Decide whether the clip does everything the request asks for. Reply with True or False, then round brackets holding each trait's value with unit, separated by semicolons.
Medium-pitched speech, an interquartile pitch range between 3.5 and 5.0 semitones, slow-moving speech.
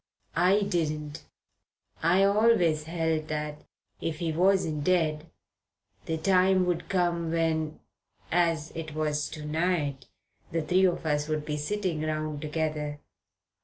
False (160 Hz; 2.6 semitones; 130 wpm)